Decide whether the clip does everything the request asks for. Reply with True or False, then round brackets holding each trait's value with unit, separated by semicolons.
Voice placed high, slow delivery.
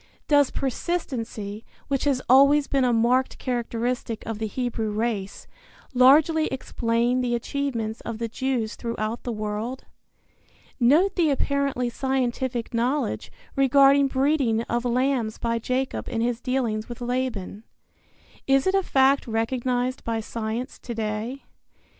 True (245 Hz; 130 wpm)